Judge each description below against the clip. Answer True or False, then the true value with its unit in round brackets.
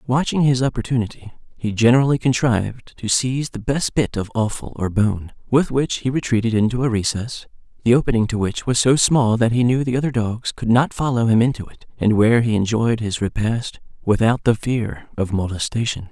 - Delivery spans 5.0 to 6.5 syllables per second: True (5.5 syllables/s)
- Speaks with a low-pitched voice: True (115 Hz)